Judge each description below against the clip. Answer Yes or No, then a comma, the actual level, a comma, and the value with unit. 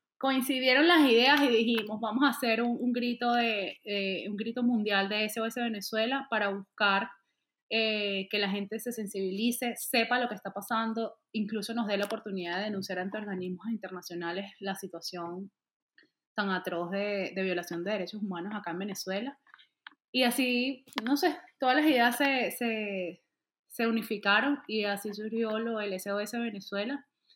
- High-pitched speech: Yes, high, 215 Hz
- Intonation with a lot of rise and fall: No, average, 3.5 semitones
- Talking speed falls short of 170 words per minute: Yes, average, 160 wpm